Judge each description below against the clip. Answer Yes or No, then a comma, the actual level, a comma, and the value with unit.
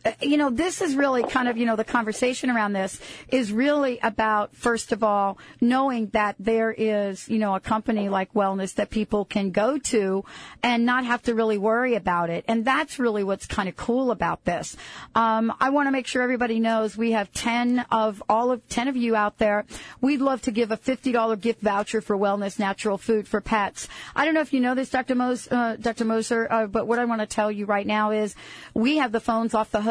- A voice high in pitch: Yes, high, 225 Hz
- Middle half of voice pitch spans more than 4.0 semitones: No, average, 2.7 semitones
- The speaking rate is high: Yes, fast, 230 wpm